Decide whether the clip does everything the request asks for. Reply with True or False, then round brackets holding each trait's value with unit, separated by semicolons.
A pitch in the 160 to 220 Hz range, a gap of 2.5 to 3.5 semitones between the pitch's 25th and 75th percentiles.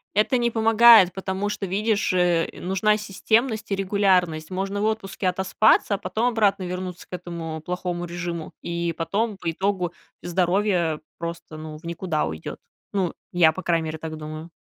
True (185 Hz; 3.2 semitones)